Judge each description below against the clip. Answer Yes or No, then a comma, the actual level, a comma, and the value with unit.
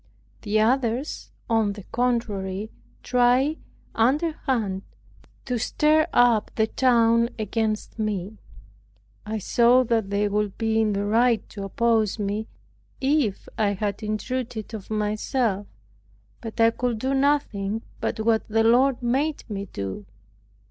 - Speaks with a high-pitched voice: Yes, high, 225 Hz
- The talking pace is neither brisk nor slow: No, slow, 130 wpm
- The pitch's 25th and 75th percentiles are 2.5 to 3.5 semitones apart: Yes, average, 2.8 semitones